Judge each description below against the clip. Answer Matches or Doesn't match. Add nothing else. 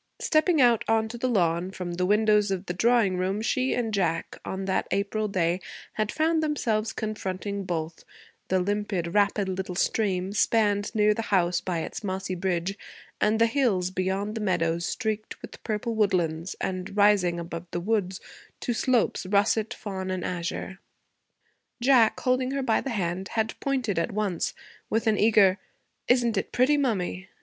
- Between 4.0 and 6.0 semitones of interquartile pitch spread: Doesn't match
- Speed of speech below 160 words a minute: Doesn't match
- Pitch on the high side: Matches